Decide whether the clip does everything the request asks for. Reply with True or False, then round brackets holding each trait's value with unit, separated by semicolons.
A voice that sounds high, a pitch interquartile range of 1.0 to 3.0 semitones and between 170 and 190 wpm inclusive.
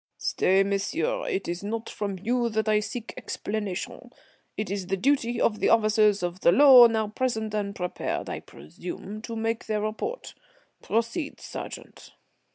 False (215 Hz; 2.7 semitones; 160 wpm)